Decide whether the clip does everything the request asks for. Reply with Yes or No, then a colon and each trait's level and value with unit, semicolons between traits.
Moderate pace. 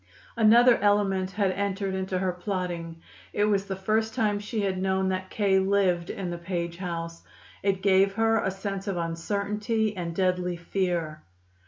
Yes: average, 165 wpm